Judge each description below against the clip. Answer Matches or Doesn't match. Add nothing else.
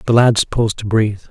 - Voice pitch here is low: Matches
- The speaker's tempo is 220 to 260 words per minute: Matches